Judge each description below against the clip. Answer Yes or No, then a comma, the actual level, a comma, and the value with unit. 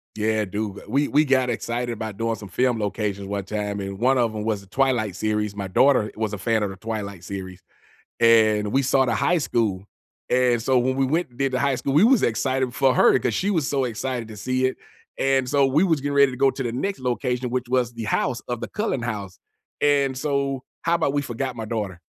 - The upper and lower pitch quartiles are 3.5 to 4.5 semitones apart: Yes, average, 4.1 semitones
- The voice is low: Yes, low, 120 Hz